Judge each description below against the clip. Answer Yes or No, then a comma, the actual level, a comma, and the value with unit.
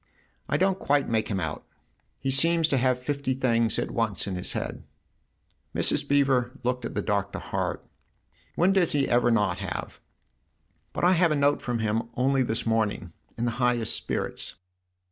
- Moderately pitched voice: No, low, 125 Hz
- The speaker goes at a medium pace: Yes, average, 185 wpm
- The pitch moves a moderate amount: Yes, average, 4.0 semitones